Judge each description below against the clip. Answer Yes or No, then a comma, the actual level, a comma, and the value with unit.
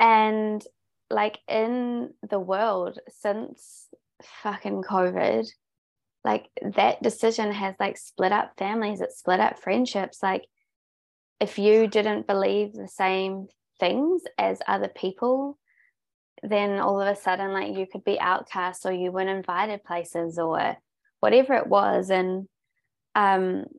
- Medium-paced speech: No, slow, 130 wpm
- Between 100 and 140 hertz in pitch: No, high, 200 Hz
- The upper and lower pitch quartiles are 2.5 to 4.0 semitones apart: Yes, average, 2.8 semitones